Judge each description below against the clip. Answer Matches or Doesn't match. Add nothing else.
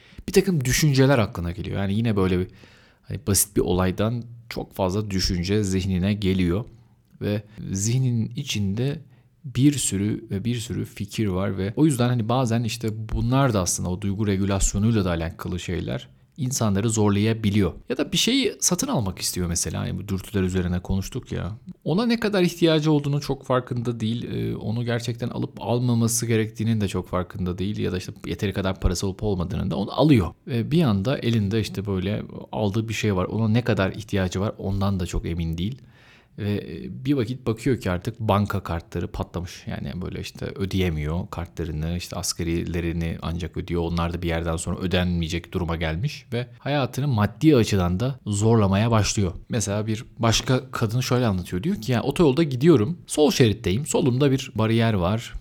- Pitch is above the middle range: Doesn't match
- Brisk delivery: Matches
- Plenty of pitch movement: Doesn't match